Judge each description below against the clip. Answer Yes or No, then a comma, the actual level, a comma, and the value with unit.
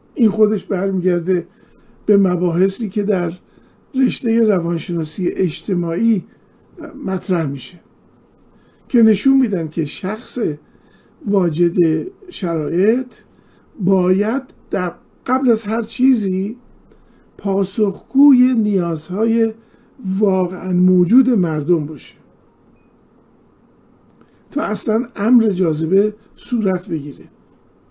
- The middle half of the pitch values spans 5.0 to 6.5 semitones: No, average, 4.2 semitones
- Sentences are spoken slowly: Yes, slow, 80 wpm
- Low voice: No, high, 200 Hz